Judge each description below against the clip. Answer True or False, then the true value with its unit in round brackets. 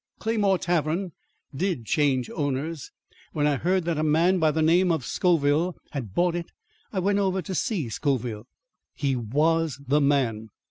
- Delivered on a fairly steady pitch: False (4.3 semitones)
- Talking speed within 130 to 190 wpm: True (165 wpm)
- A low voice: False (155 Hz)